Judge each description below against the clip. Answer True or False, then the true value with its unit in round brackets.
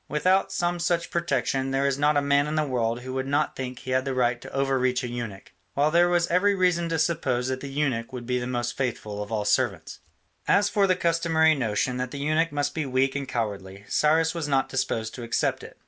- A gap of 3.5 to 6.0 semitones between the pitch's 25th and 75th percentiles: True (4.4 semitones)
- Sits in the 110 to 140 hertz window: True (135 Hz)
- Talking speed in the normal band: False (240 wpm)